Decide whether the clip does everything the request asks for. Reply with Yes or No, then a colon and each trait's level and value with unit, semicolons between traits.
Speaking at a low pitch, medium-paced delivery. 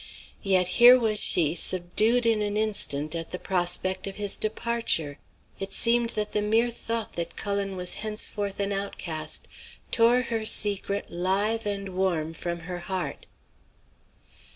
No: high, 200 Hz; average, 145 wpm